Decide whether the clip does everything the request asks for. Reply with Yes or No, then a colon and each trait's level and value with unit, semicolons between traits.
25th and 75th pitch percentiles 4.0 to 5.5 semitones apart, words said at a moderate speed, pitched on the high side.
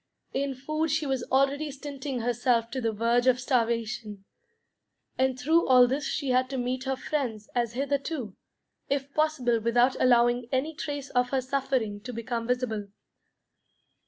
No: narrow, 2.6 semitones; average, 155 wpm; very high, 255 Hz